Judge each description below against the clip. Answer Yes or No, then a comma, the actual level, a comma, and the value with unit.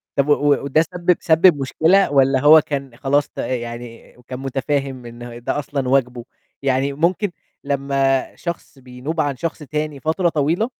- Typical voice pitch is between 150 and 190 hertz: No, medium, 140 Hz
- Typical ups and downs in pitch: Yes, average, 3.2 semitones